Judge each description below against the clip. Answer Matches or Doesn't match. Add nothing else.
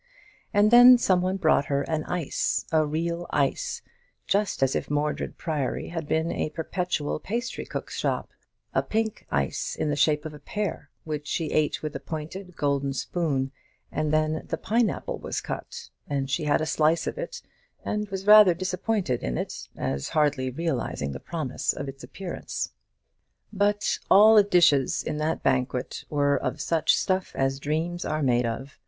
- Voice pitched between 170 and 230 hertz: Doesn't match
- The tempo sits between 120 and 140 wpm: Doesn't match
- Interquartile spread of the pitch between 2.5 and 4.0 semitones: Doesn't match